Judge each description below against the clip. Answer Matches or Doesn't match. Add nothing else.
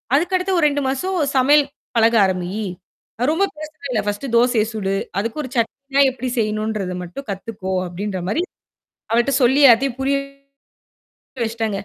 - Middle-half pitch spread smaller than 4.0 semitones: Doesn't match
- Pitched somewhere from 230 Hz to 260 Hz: Matches